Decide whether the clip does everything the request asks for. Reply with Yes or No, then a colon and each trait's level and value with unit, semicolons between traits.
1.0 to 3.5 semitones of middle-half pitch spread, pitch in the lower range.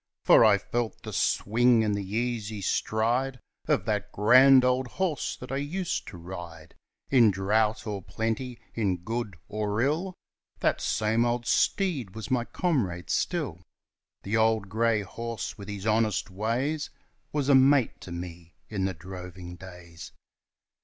No: average, 4.5 semitones; low, 110 Hz